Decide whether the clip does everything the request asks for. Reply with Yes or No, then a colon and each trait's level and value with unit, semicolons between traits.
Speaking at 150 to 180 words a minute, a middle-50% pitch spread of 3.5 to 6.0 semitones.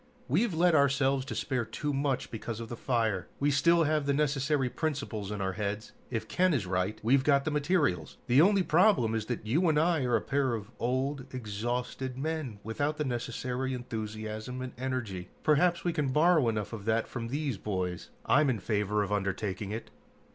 No: average, 190 wpm; average, 5.1 semitones